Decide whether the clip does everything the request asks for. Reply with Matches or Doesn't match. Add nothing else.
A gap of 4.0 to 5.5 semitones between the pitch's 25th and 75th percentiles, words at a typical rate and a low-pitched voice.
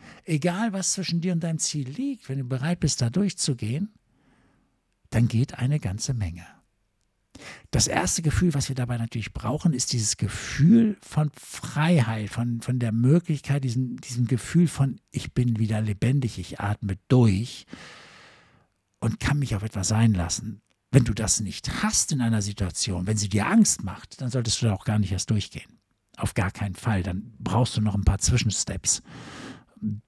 Matches